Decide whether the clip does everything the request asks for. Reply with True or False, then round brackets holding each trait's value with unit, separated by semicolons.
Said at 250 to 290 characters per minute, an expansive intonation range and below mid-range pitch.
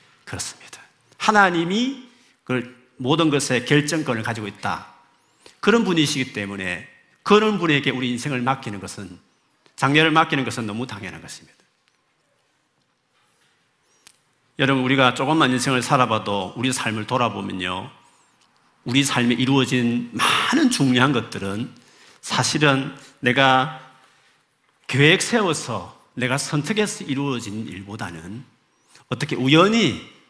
False (265 characters per minute; 4.3 semitones; 130 Hz)